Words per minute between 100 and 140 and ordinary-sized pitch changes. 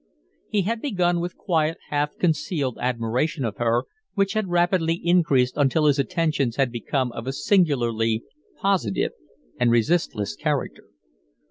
No: slow, 135 wpm; wide, 6.2 semitones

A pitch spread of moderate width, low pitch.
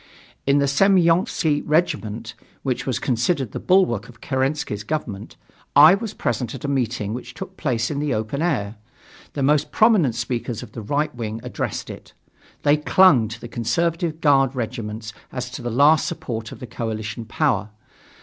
Yes: average, 4.9 semitones; low, 130 Hz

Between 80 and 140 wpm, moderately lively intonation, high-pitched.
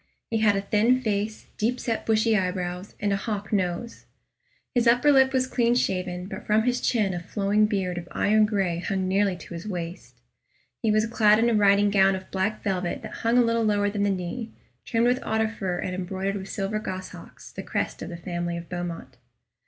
No: fast, 205 wpm; average, 3.2 semitones; high, 205 Hz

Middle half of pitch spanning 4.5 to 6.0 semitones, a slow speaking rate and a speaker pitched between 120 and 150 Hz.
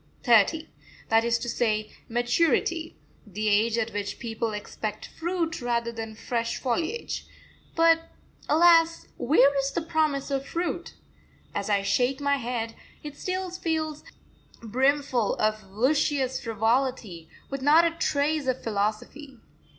No: wide, 5.6 semitones; slow, 130 wpm; very high, 260 Hz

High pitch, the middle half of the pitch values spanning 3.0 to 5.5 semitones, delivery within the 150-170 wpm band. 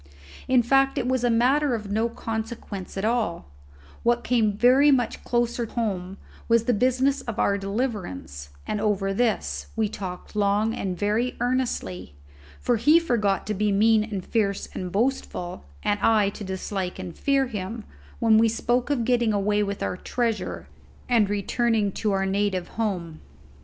Yes: high, 215 Hz; average, 3.4 semitones; average, 165 wpm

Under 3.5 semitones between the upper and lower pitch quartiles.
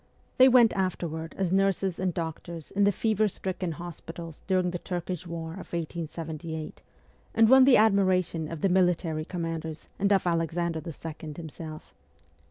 Yes: average, 2.8 semitones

